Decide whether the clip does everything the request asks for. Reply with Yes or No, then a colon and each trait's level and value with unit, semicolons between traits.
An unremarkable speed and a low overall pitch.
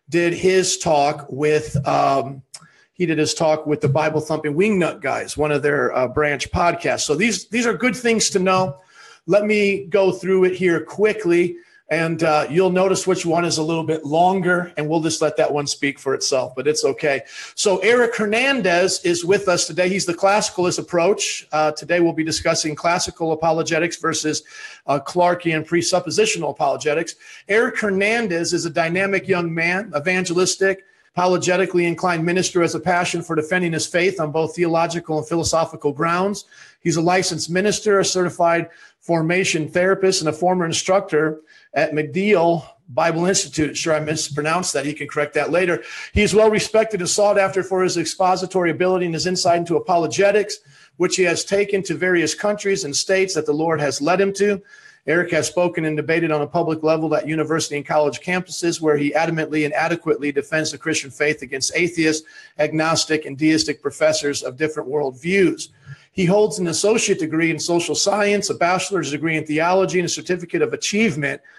No: average, 180 wpm; medium, 170 Hz